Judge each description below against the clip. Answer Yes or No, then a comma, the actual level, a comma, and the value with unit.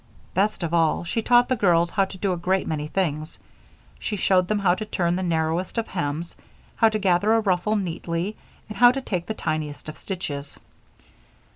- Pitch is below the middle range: No, medium, 185 Hz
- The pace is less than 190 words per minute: No, average, 195 wpm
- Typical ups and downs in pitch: Yes, average, 3.9 semitones